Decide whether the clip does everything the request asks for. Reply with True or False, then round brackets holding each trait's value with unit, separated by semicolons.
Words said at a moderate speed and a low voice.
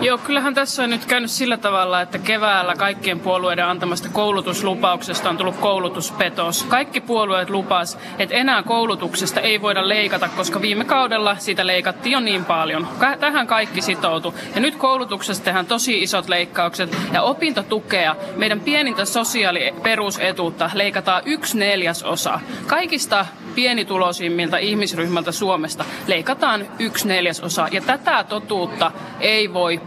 False (130 wpm; 195 Hz)